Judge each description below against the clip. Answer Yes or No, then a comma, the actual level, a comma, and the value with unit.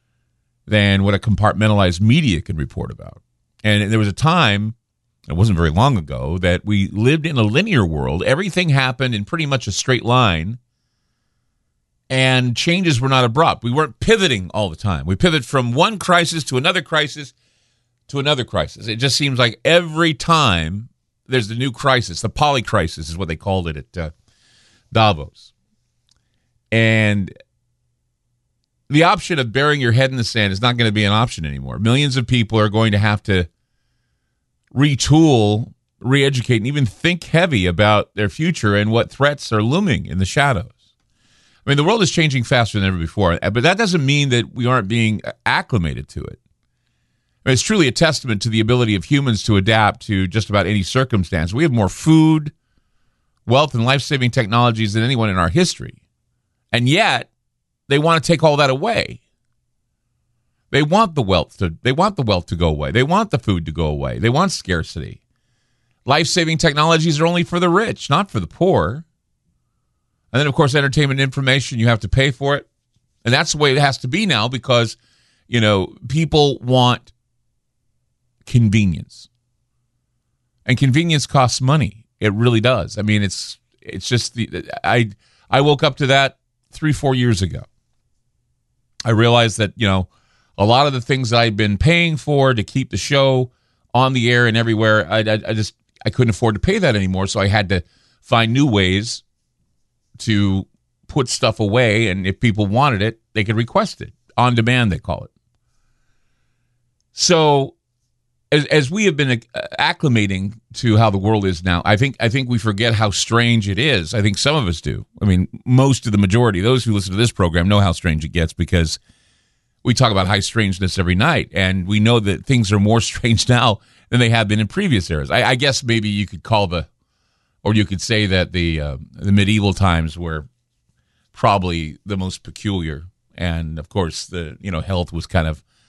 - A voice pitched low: Yes, low, 115 Hz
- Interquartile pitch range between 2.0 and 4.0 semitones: No, average, 4.6 semitones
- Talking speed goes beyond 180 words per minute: Yes, average, 190 wpm